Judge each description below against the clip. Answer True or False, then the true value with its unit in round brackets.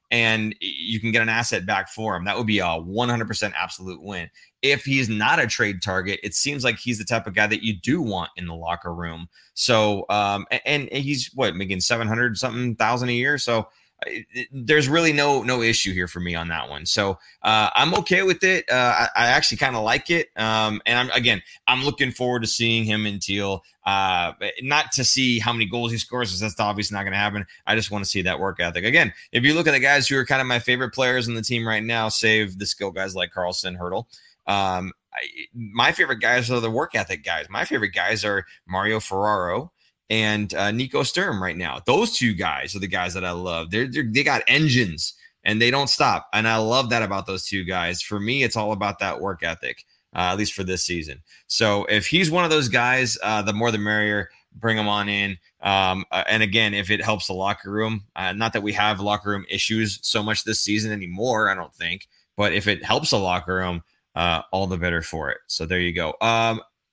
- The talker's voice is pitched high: False (110 Hz)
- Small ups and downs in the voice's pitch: False (3.7 semitones)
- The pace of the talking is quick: True (235 wpm)